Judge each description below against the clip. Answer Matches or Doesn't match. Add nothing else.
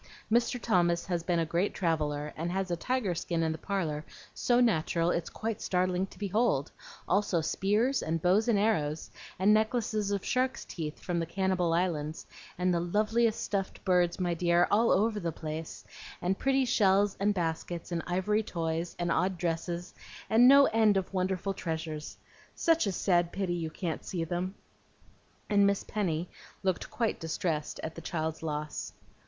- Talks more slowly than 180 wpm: Matches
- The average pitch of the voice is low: Doesn't match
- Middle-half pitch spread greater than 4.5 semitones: Doesn't match